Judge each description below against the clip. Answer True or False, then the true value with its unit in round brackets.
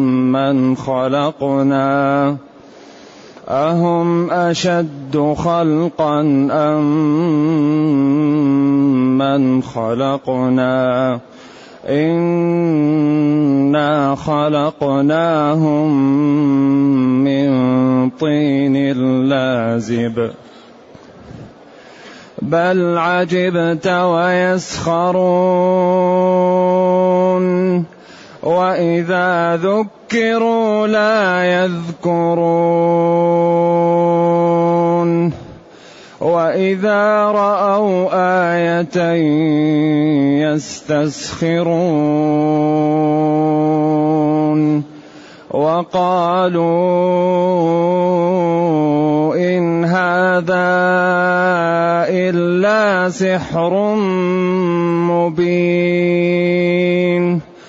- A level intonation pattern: False (3.2 semitones)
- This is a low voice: False (170 Hz)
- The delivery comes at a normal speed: False (30 wpm)